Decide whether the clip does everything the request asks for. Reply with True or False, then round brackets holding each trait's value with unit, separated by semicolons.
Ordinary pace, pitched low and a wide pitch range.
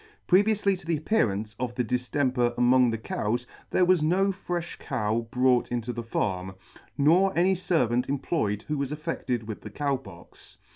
True (165 wpm; 125 Hz; 6.2 semitones)